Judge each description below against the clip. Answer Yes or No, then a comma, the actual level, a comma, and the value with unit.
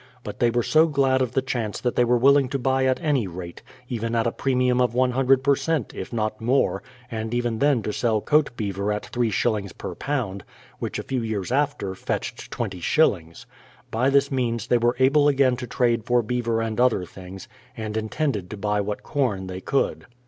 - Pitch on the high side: No, low, 120 Hz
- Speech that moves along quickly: Yes, fast, 215 wpm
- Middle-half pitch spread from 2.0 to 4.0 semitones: Yes, average, 3.6 semitones